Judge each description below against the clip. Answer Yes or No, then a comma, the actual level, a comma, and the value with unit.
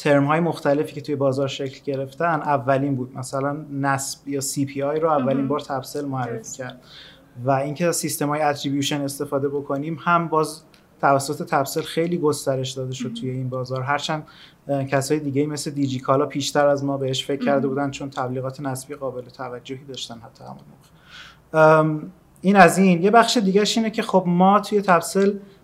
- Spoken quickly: Yes, fast, 175 wpm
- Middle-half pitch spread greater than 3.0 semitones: No, narrow, 2.6 semitones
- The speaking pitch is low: No, medium, 145 Hz